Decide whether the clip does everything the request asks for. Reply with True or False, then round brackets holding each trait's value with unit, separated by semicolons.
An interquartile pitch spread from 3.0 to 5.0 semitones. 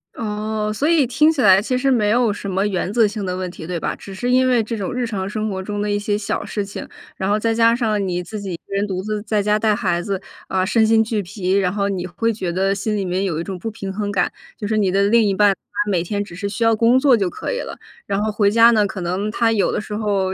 False (2.5 semitones)